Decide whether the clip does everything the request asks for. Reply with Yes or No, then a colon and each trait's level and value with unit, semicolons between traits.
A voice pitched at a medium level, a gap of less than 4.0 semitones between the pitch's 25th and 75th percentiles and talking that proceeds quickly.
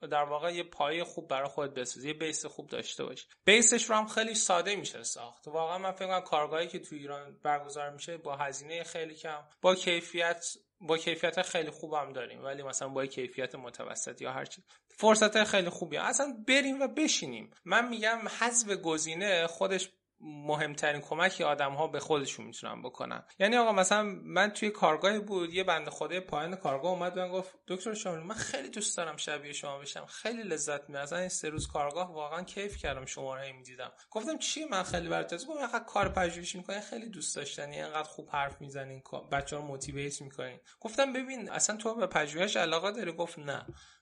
No: medium, 170 Hz; wide, 5.5 semitones; fast, 190 wpm